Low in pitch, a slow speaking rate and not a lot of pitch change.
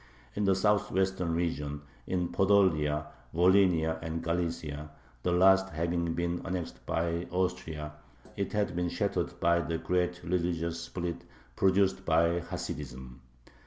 Yes: very low, 85 Hz; slow, 125 wpm; narrow, 2.1 semitones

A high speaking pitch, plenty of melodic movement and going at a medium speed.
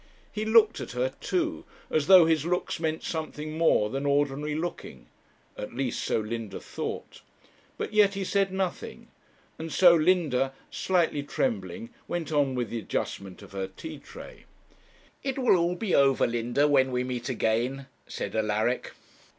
No: medium, 150 Hz; wide, 6.3 semitones; average, 160 wpm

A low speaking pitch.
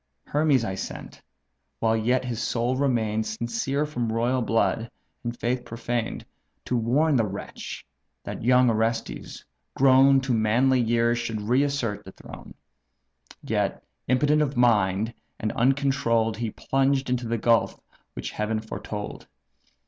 Yes: low, 120 Hz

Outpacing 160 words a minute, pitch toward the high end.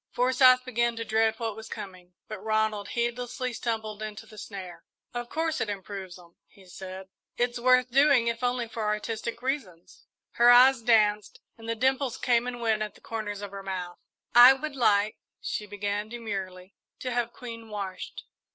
Yes: average, 175 wpm; high, 225 Hz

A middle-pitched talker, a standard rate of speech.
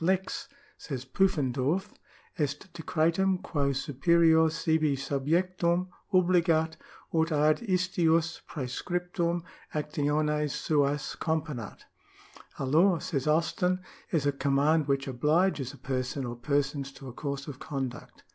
No: medium, 155 Hz; slow, 120 wpm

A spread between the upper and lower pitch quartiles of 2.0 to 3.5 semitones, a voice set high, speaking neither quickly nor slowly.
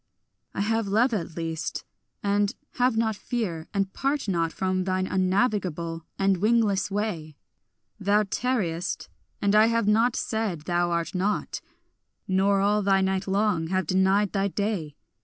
Yes: narrow, 2.6 semitones; high, 195 Hz; average, 145 wpm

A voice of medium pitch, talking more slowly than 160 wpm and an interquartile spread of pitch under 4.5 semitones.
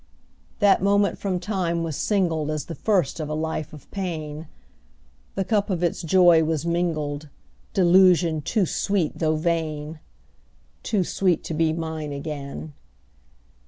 Yes: medium, 165 Hz; average, 150 wpm; average, 3.2 semitones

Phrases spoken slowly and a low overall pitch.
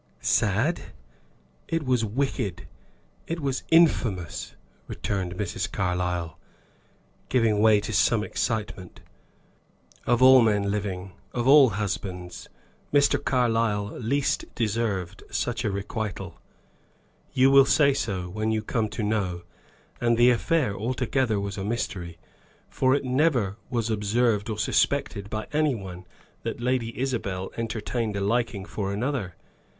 Yes: slow, 125 wpm; low, 110 Hz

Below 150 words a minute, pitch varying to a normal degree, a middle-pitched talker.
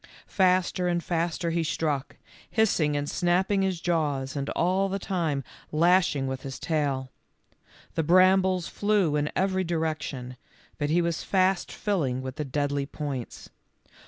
Yes: average, 140 wpm; average, 4.3 semitones; medium, 165 Hz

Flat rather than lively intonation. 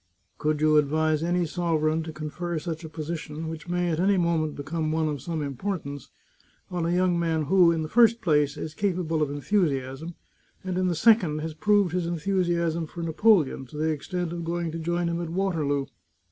Yes: narrow, 2.3 semitones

